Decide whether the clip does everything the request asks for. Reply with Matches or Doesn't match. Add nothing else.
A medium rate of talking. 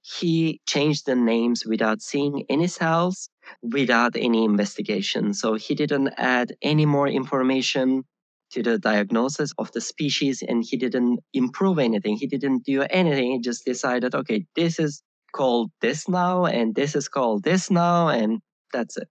Matches